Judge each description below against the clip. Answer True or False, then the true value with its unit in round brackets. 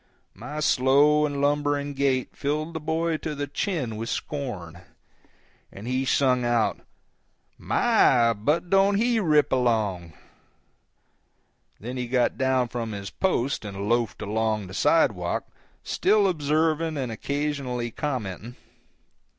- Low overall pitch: True (130 Hz)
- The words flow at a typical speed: False (125 wpm)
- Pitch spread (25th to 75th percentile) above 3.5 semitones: True (4.6 semitones)